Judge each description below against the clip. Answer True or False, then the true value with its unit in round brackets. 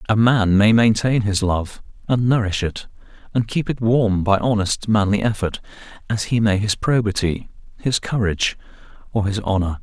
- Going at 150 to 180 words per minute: True (165 wpm)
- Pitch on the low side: True (105 Hz)